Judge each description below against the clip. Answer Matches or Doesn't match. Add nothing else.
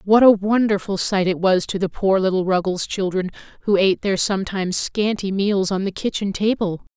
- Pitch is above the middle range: Matches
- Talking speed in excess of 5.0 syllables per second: Matches